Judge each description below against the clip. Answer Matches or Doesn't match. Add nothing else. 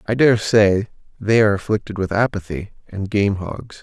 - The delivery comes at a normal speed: Matches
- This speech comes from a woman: Doesn't match